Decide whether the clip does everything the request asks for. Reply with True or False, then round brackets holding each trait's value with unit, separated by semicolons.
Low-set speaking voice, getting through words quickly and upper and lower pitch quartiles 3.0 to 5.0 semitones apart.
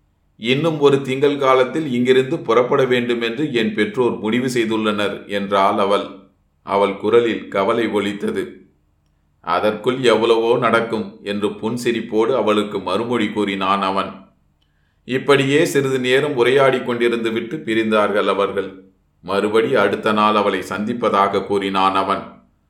False (105 Hz; 110 wpm; 3.7 semitones)